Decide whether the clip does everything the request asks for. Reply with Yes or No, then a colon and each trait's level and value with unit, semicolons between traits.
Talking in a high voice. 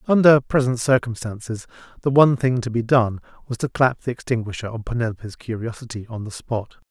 No: low, 120 Hz